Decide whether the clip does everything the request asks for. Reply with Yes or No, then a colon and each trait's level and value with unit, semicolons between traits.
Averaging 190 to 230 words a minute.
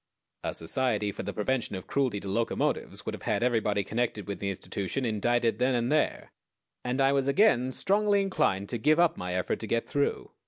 Yes: average, 200 wpm